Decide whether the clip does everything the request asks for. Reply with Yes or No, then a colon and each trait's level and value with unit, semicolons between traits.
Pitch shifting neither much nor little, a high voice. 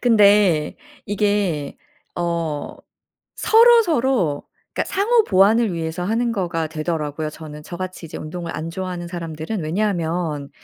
No: average, 4.6 semitones; medium, 175 Hz